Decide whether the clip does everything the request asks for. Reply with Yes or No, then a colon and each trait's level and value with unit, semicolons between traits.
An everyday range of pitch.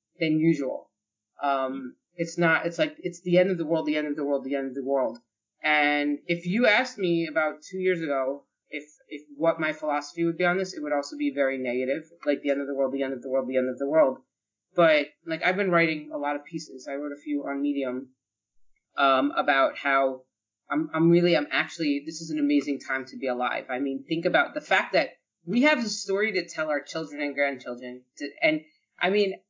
Yes: average, 3.8 semitones